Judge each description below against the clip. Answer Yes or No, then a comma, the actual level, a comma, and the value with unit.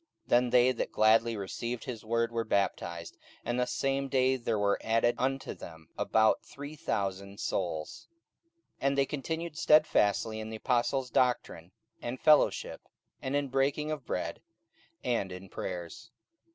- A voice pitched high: No, low, 120 Hz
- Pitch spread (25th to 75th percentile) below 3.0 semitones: No, average, 4.8 semitones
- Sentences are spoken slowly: No, average, 150 wpm